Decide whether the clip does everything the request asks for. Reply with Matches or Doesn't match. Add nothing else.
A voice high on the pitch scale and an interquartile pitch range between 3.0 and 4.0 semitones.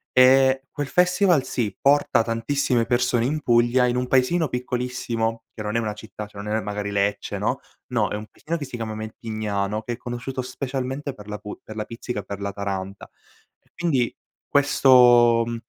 Doesn't match